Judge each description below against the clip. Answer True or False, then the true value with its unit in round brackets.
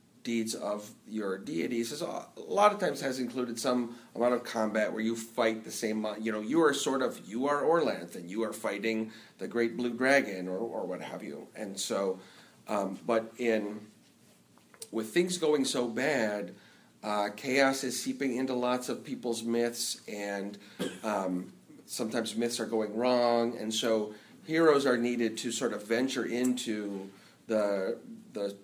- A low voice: True (115 Hz)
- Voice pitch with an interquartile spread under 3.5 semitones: True (2.7 semitones)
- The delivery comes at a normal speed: True (165 wpm)